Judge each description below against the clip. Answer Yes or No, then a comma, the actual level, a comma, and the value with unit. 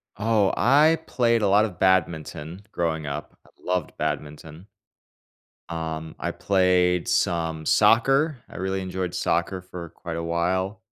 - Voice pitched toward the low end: Yes, very low, 90 Hz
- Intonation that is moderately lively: Yes, average, 3.5 semitones